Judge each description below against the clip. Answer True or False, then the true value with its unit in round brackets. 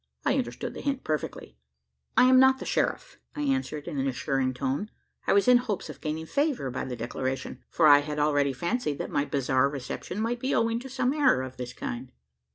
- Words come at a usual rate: False (210 wpm)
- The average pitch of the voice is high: False (150 Hz)